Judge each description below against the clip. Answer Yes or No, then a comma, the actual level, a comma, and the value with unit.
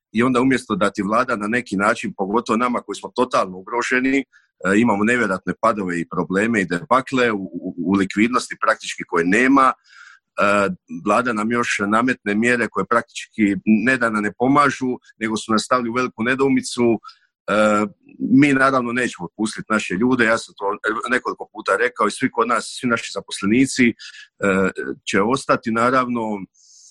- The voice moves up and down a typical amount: Yes, average, 3.6 semitones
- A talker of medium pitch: No, low, 115 Hz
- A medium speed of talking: Yes, average, 150 wpm